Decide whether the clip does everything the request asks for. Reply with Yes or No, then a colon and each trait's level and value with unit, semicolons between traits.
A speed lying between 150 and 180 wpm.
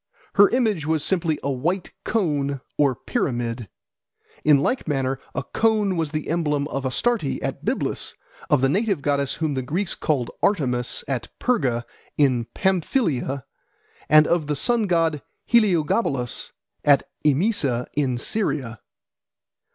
No: slow, 135 wpm